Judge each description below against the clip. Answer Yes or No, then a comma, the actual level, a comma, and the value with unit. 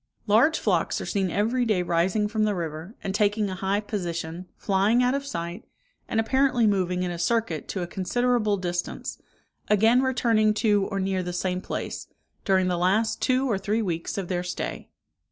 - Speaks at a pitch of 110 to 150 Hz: No, high, 200 Hz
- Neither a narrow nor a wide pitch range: Yes, average, 3.7 semitones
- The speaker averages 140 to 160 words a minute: No, average, 185 wpm